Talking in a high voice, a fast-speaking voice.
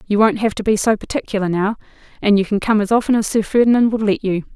Yes: high, 210 Hz; fast, 265 wpm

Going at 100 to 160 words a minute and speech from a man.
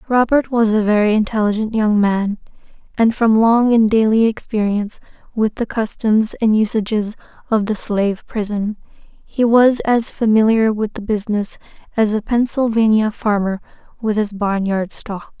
No: average, 150 wpm; female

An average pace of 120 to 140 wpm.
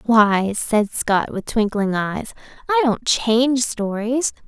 Yes: slow, 135 wpm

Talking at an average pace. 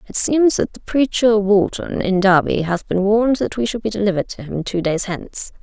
No: fast, 225 wpm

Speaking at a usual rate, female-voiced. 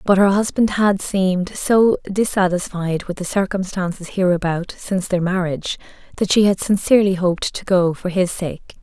Yes: average, 165 wpm; female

